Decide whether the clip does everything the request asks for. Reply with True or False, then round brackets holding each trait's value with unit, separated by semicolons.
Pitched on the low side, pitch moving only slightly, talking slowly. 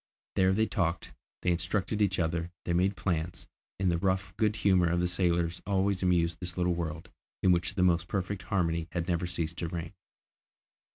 False (90 Hz; 1.8 semitones; 185 wpm)